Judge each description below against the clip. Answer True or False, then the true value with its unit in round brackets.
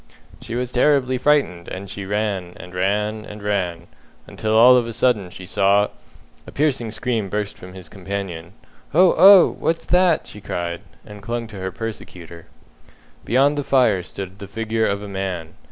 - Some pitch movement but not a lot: True (4.4 semitones)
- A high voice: False (105 Hz)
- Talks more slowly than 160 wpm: False (175 wpm)